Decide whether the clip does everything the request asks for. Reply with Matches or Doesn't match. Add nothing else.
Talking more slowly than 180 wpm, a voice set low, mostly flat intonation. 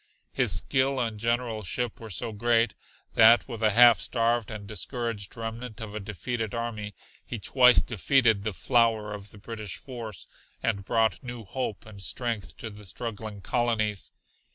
Matches